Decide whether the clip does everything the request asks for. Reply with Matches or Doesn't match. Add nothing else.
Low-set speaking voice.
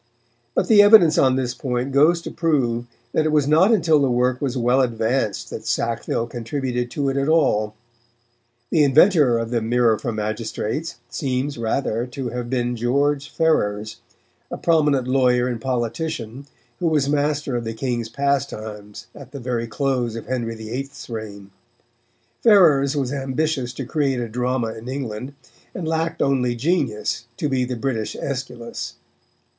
Matches